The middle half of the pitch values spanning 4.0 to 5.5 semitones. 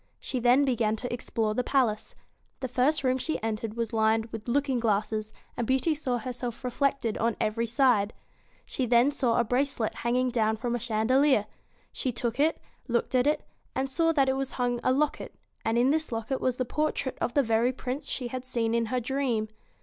No: average, 2.7 semitones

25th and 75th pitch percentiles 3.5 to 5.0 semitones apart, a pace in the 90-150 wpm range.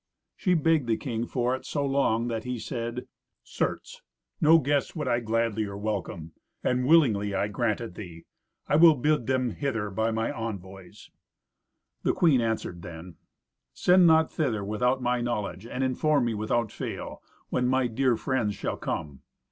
No: average, 3.8 semitones; average, 165 wpm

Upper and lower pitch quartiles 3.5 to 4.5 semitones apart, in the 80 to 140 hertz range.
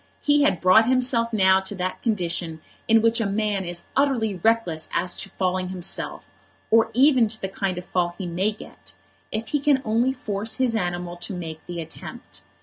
No: average, 4.2 semitones; high, 200 Hz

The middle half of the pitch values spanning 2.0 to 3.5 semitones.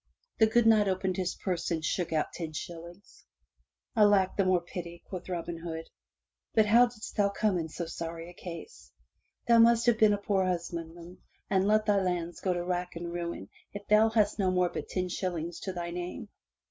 Yes: average, 3.2 semitones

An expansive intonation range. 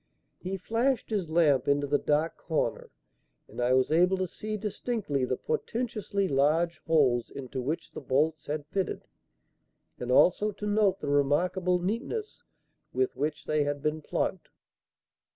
Yes: wide, 5.7 semitones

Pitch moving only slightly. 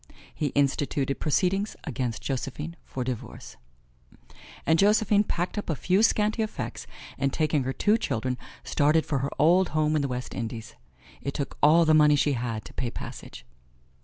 No: average, 4.9 semitones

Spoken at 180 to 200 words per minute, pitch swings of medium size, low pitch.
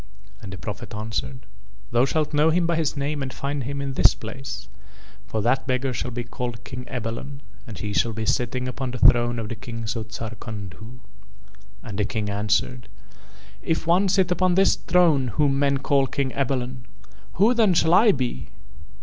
Yes: average, 185 wpm; average, 4.1 semitones; low, 125 Hz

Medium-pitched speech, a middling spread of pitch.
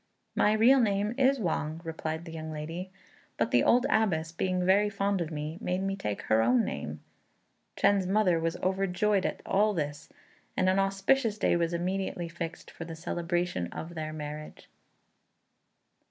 Yes: medium, 175 Hz; average, 3.7 semitones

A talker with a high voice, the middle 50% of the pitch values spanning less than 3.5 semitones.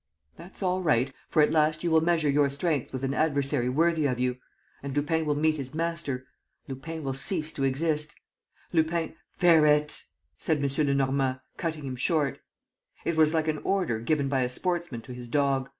No: medium, 150 Hz; average, 3.1 semitones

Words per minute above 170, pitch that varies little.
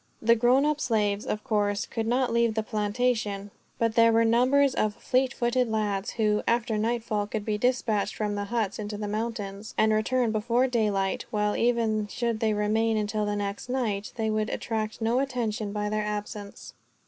Yes: average, 185 wpm; narrow, 2.1 semitones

